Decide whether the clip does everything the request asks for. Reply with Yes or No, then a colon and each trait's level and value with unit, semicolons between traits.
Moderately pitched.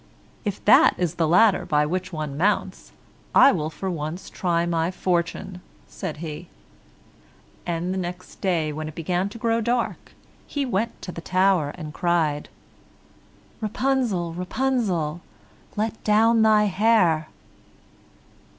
Yes: medium, 180 Hz